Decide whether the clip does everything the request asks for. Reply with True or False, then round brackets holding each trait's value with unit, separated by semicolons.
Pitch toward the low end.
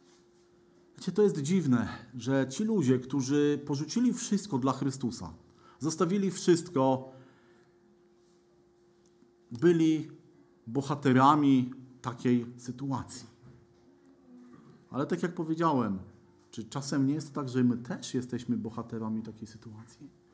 True (130 Hz)